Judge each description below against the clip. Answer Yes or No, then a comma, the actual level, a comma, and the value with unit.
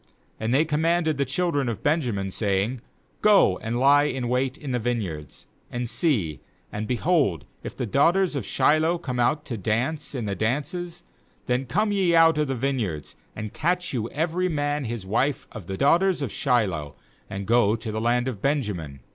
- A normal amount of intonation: No, wide, 6.1 semitones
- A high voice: No, low, 130 Hz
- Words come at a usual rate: Yes, average, 180 wpm